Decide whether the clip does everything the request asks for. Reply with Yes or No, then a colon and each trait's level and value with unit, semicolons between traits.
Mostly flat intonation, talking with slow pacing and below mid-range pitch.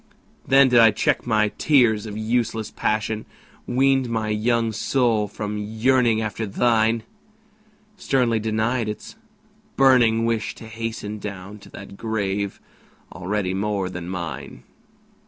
Yes: narrow, 2.0 semitones; slow, 125 wpm; low, 110 Hz